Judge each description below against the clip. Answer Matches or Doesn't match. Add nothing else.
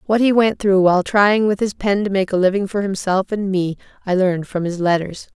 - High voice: Matches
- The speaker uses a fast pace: Matches